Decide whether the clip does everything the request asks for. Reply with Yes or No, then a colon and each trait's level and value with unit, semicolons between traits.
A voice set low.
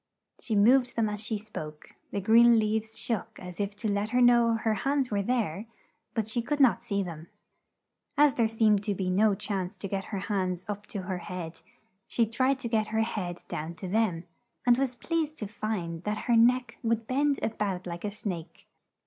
No: high, 215 Hz